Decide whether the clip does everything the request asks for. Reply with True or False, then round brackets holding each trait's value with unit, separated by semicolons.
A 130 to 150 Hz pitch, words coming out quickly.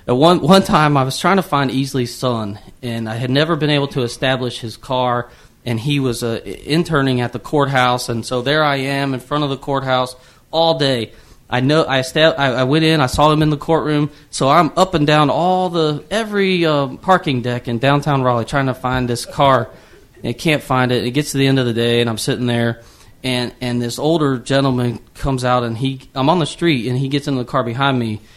True (135 Hz; 235 wpm)